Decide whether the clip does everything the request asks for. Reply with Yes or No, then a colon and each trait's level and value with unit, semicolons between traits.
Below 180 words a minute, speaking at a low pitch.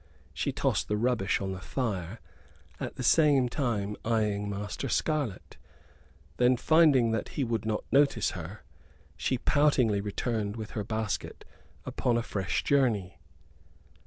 Yes: slow, 135 wpm; low, 115 Hz